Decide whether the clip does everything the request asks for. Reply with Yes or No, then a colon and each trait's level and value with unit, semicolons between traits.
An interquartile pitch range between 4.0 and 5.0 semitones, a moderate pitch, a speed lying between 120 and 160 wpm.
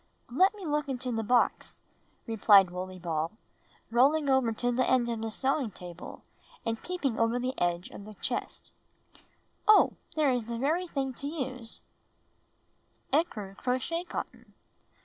No: average, 4.4 semitones; high, 245 Hz; average, 150 wpm